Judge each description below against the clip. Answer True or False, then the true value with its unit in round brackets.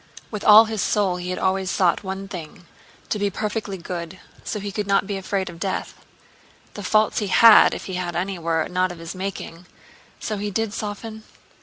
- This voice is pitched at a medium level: False (195 Hz)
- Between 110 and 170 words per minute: False (180 wpm)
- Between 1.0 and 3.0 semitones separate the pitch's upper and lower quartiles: True (2.5 semitones)